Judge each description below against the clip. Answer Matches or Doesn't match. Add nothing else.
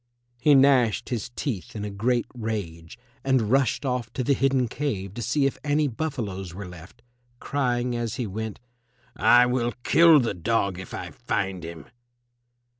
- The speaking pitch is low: Matches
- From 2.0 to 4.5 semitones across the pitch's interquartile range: Doesn't match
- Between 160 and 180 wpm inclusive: Matches